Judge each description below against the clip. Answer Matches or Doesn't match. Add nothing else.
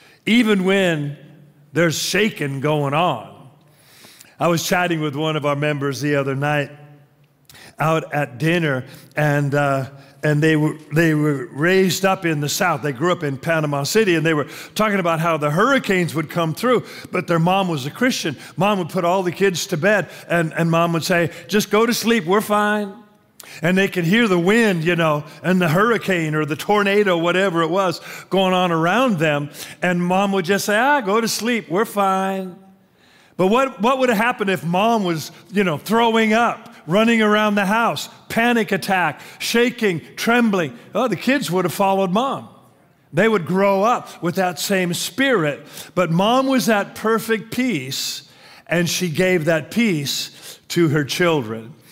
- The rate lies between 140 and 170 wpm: Doesn't match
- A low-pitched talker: Doesn't match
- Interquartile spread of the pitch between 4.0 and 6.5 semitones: Matches